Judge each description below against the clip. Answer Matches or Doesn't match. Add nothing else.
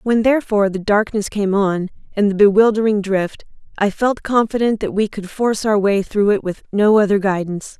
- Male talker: Doesn't match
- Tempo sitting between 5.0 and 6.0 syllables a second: Matches